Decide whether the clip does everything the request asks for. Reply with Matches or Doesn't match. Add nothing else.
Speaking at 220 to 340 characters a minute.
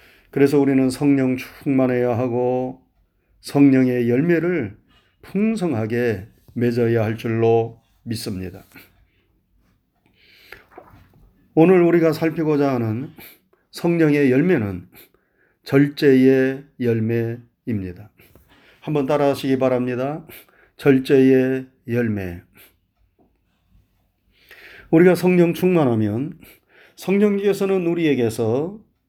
Doesn't match